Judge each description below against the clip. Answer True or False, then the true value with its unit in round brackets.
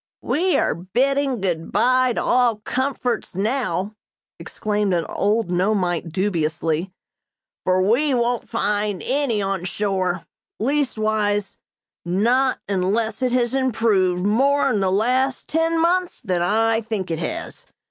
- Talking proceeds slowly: True (125 wpm)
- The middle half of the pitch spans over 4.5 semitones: True (5.3 semitones)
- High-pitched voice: True (215 Hz)